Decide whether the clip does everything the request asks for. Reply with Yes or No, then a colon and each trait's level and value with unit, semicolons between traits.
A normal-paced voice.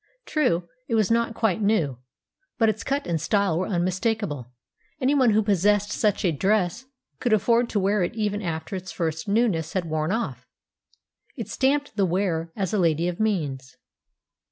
Yes: average, 170 wpm